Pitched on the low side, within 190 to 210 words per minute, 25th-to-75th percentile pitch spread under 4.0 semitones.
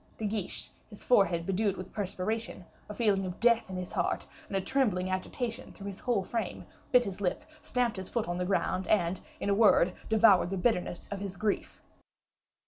No: high, 200 Hz; average, 195 wpm; average, 3.2 semitones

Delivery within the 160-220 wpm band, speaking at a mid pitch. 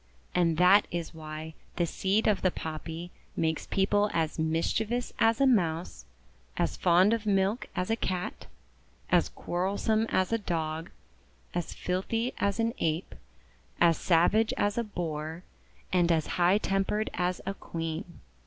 No: average, 145 wpm; medium, 180 Hz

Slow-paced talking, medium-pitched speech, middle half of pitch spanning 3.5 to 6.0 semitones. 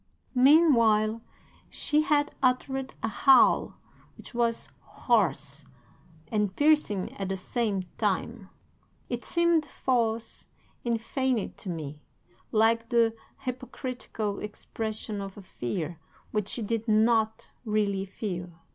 No: slow, 110 wpm; high, 225 Hz; average, 3.8 semitones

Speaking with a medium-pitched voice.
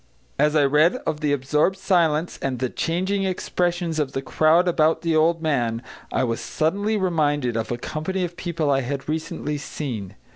Yes: medium, 155 Hz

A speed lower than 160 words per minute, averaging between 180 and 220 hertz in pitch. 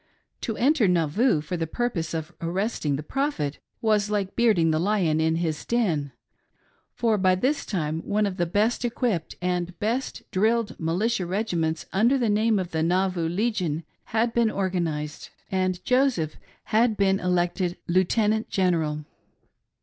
Yes: average, 150 wpm; medium, 185 Hz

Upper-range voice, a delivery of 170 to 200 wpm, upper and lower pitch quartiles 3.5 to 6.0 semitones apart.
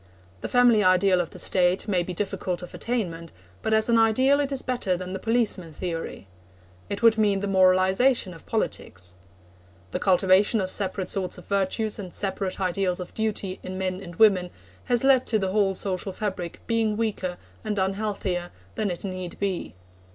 No: high, 195 Hz; average, 180 wpm; average, 3.0 semitones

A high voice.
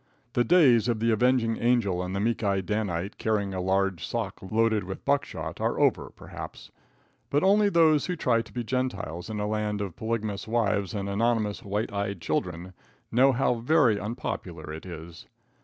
No: low, 110 Hz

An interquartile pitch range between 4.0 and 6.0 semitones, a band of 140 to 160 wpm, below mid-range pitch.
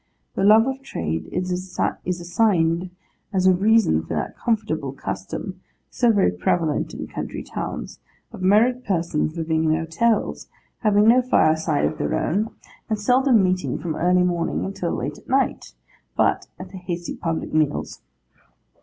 No: average, 5.1 semitones; average, 150 wpm; medium, 180 Hz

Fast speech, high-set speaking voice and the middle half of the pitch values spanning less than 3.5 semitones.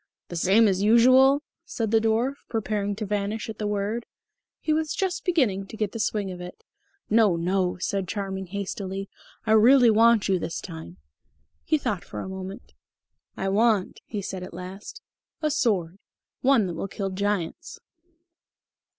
No: average, 170 wpm; high, 205 Hz; average, 3.1 semitones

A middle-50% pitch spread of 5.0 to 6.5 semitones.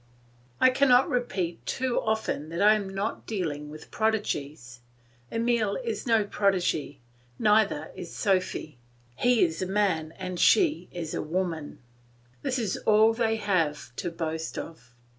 Yes: wide, 5.4 semitones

